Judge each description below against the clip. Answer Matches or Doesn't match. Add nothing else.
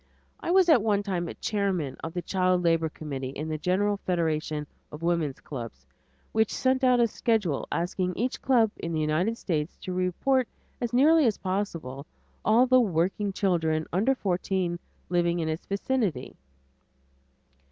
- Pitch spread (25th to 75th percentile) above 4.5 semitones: Matches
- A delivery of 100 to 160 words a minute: Matches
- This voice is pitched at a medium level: Matches